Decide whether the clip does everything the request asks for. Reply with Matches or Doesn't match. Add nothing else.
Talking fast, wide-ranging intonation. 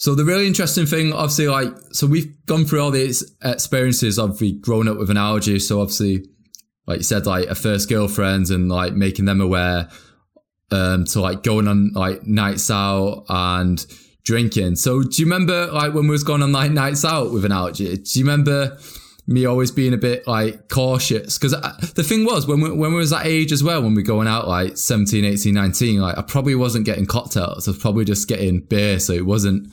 Matches